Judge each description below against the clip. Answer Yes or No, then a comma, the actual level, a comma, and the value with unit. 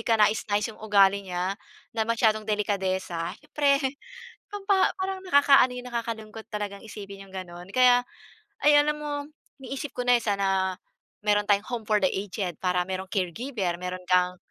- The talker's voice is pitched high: Yes, high, 210 Hz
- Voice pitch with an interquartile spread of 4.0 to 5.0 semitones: Yes, average, 4.6 semitones